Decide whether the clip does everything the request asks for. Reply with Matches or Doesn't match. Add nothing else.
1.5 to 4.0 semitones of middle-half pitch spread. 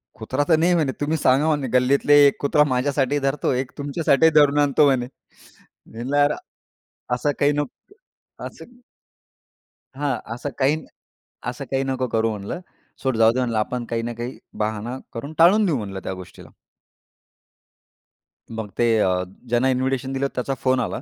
Matches